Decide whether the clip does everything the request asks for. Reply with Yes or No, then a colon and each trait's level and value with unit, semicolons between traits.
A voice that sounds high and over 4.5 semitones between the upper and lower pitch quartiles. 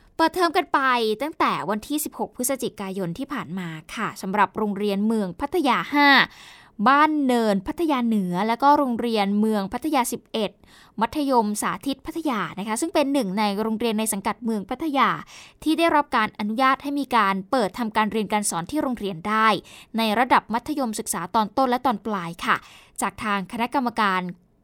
Yes: high, 230 Hz; average, 4.9 semitones